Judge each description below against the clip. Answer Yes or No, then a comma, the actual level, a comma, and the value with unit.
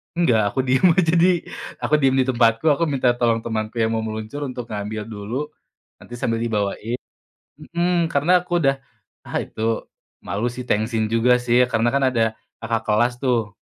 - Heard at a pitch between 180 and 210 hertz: No, low, 120 Hz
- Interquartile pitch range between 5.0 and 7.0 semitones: No, average, 3.5 semitones